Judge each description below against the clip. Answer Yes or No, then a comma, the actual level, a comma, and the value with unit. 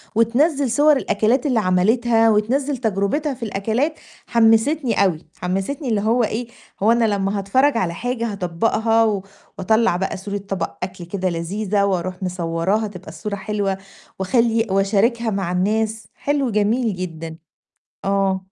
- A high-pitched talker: Yes, high, 210 Hz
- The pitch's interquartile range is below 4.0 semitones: Yes, average, 3.5 semitones